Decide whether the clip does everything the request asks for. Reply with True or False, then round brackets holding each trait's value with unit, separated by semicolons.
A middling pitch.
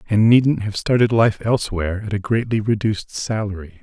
False (105 Hz)